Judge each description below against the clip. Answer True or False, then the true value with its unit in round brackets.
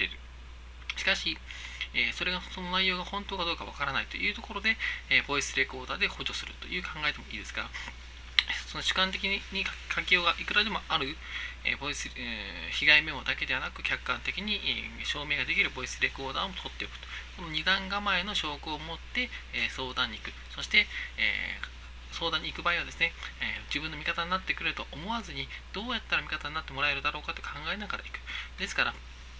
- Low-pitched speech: False (150 Hz)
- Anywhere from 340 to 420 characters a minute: True (390 characters per minute)